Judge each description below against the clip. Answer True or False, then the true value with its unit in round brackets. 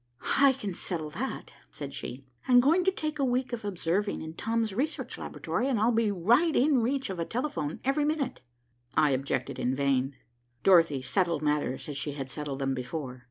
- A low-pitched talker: False (190 Hz)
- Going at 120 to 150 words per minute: False (195 wpm)